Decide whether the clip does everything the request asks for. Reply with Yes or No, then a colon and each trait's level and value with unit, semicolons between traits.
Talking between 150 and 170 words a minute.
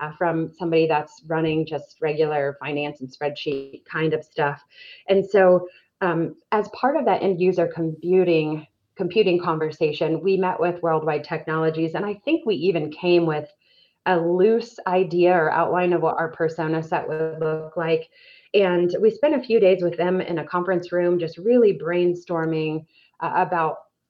Yes: average, 165 wpm